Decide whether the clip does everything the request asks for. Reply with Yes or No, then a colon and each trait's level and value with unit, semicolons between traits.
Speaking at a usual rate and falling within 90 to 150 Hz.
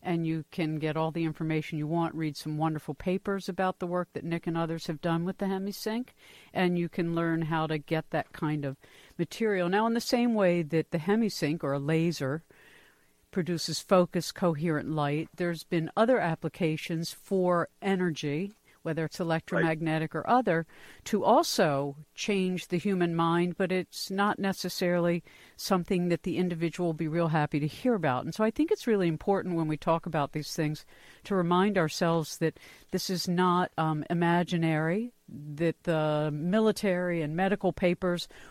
No: average, 175 wpm; medium, 170 Hz